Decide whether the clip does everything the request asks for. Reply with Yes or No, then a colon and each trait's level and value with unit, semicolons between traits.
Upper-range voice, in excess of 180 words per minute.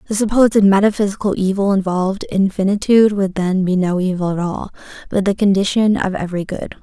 No: high, 195 Hz; average, 175 wpm